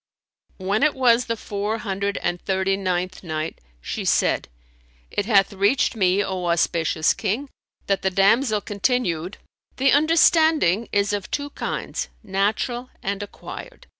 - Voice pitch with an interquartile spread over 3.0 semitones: Yes, average, 4.2 semitones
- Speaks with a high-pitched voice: Yes, high, 200 Hz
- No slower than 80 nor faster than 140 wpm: Yes, slow, 135 wpm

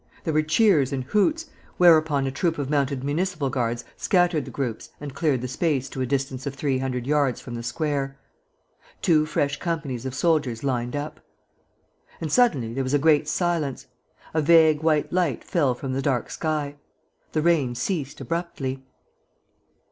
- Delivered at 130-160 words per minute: No, average, 170 wpm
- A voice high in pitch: No, medium, 145 Hz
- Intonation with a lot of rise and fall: No, average, 3.4 semitones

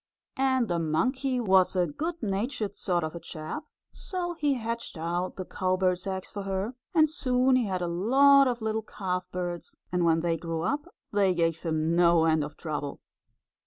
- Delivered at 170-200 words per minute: Yes, average, 180 wpm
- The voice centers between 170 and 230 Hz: Yes, high, 190 Hz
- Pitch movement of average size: No, wide, 6.7 semitones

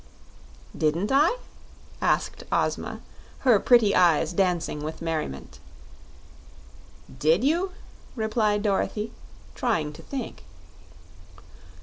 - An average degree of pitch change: No, wide, 6.7 semitones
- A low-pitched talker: No, high, 200 Hz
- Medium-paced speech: No, slow, 85 wpm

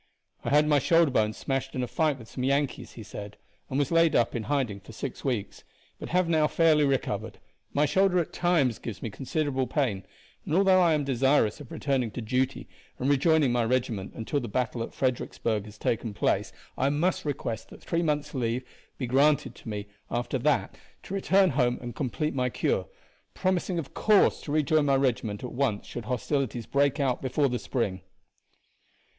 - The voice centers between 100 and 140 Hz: Yes, low, 135 Hz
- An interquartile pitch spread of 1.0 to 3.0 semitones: No, average, 4.1 semitones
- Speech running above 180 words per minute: Yes, average, 190 wpm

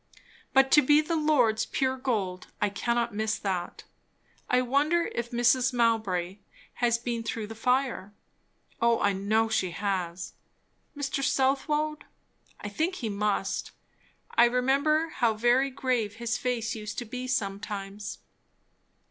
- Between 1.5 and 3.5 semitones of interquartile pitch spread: No, average, 4.1 semitones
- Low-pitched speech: No, high, 235 Hz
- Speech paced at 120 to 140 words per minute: Yes, slow, 135 wpm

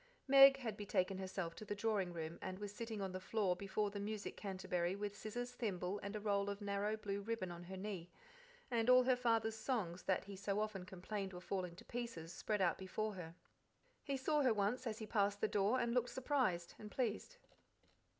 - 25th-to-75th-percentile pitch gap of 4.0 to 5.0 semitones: No, average, 3.1 semitones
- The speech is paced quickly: Yes, fast, 210 wpm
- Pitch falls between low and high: No, high, 205 Hz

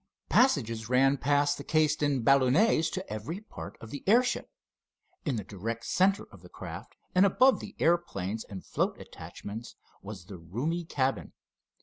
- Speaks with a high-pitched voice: No, medium, 140 Hz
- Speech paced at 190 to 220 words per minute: No, average, 155 wpm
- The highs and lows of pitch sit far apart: Yes, wide, 7.4 semitones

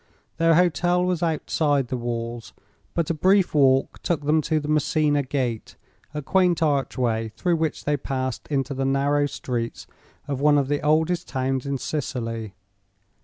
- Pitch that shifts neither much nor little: Yes, average, 3.3 semitones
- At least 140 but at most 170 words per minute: Yes, average, 160 wpm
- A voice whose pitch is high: No, medium, 145 Hz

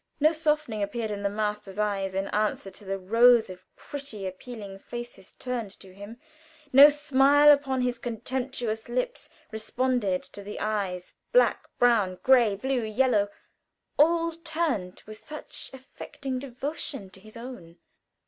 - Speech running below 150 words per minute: Yes, average, 140 wpm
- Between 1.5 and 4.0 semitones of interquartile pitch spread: No, average, 4.8 semitones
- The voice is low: No, high, 235 Hz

